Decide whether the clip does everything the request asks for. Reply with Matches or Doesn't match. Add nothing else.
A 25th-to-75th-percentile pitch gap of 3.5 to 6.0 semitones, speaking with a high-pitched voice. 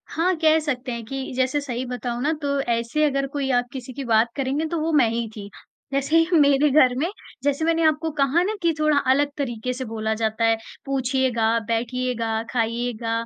Matches